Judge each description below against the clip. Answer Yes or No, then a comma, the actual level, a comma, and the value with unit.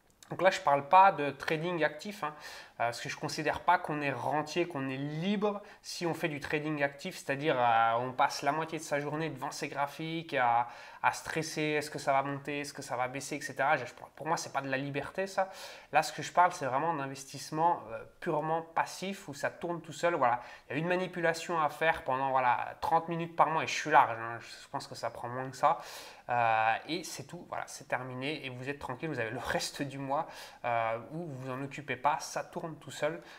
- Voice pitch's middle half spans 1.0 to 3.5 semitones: Yes, average, 3.2 semitones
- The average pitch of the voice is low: No, medium, 145 Hz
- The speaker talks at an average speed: No, fast, 240 wpm